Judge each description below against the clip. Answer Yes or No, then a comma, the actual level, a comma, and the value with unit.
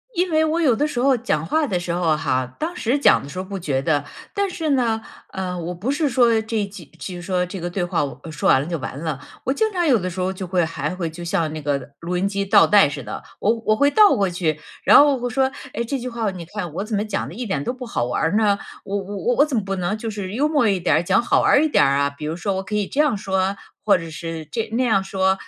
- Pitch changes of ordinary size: No, wide, 6.1 semitones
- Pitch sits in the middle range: No, high, 195 Hz